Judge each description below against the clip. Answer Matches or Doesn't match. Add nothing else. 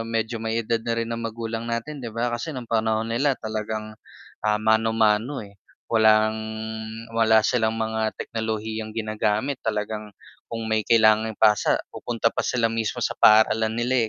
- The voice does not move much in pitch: Matches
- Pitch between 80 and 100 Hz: Doesn't match